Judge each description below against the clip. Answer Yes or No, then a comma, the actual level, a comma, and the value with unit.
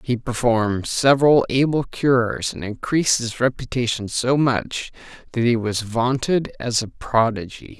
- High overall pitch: No, low, 120 Hz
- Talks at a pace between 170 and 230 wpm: No, average, 140 wpm